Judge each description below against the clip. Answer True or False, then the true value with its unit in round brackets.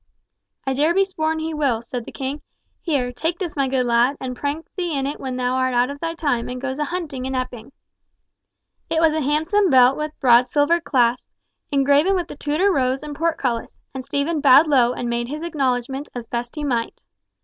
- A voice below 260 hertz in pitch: False (275 Hz)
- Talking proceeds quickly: True (215 wpm)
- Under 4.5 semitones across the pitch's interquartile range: True (3.8 semitones)